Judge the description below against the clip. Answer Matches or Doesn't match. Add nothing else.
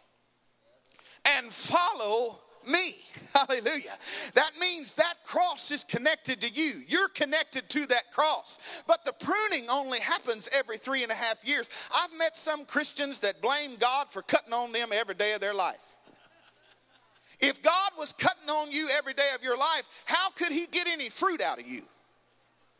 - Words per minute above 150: Matches